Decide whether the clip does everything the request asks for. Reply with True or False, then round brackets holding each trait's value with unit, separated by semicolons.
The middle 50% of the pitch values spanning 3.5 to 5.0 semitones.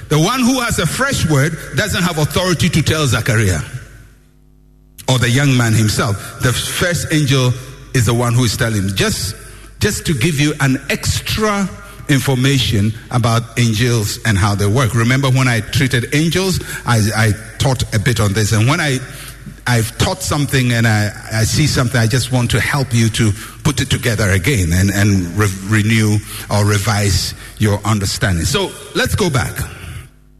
True (4.0 semitones)